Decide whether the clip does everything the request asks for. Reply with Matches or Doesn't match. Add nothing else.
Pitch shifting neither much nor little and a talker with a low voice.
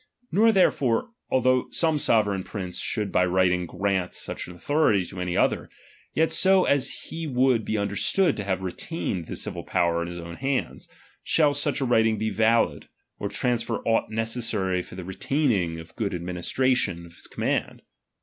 Doesn't match